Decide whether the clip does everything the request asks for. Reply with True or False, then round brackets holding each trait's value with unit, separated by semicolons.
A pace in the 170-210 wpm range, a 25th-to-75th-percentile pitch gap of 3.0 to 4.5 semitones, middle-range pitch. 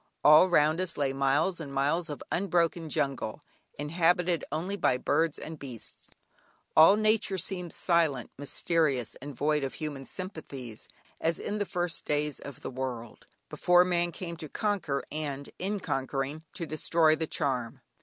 False (155 wpm; 4.0 semitones; 155 Hz)